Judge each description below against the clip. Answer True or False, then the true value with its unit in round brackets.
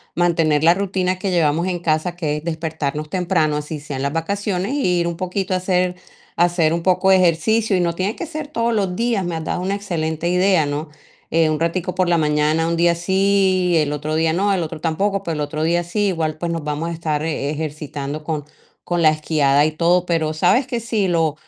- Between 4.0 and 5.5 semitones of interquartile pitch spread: False (3.1 semitones)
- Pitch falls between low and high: True (170 Hz)